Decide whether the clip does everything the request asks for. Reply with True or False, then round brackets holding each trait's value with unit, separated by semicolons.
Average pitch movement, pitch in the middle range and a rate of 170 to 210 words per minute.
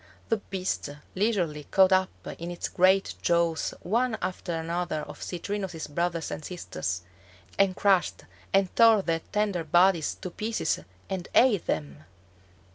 False (3.1 semitones; 180 Hz; 135 wpm)